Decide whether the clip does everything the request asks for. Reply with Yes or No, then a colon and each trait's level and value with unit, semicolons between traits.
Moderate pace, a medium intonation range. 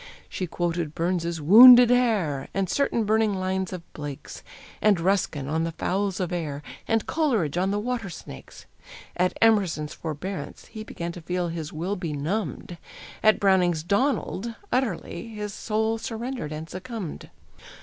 Yes: average, 145 wpm; average, 4.7 semitones